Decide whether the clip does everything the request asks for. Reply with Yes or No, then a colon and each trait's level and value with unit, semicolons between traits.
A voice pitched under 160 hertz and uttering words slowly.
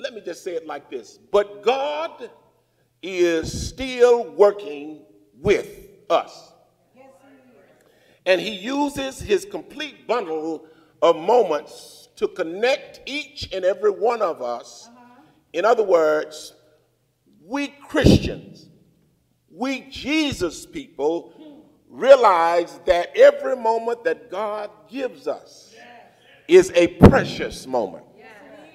No: high, 245 Hz; slow, 105 wpm